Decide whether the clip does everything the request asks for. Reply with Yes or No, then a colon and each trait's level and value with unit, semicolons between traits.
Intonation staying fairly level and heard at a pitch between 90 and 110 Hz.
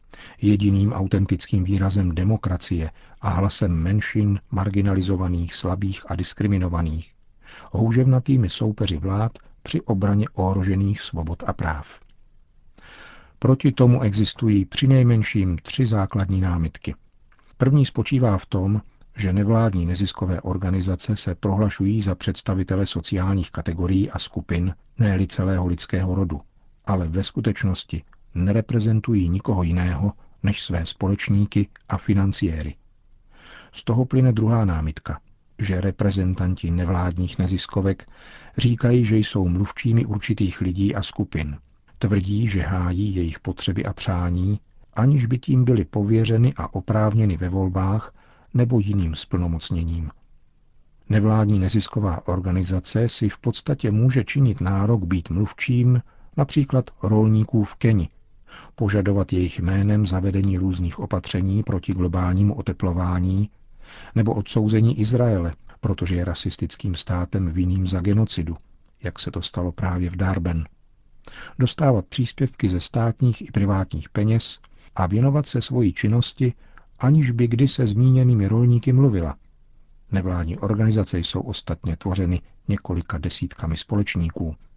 No: average, 3.5 semitones; low, 100 Hz